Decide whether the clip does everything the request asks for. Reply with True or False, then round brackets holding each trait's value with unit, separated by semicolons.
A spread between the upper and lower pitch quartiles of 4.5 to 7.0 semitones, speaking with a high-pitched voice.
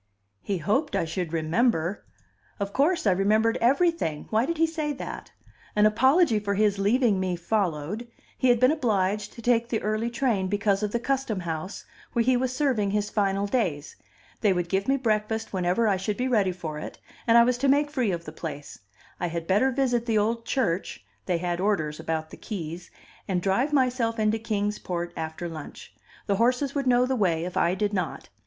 True (5.2 semitones; 210 Hz)